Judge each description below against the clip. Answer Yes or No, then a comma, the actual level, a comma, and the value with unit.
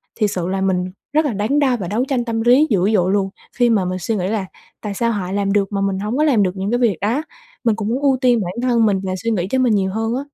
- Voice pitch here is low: No, high, 210 Hz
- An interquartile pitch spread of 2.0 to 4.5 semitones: Yes, average, 3.9 semitones